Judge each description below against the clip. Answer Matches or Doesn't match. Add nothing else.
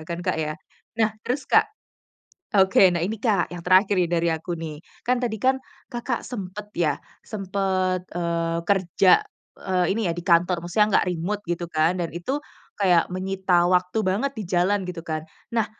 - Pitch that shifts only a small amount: Doesn't match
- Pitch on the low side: Doesn't match